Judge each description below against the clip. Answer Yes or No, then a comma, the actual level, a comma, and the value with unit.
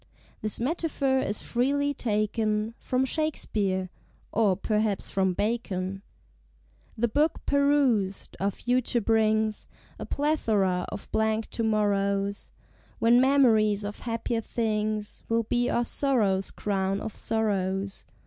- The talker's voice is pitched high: Yes, high, 220 Hz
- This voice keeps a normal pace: No, slow, 115 wpm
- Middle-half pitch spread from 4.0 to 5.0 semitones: No, average, 3.3 semitones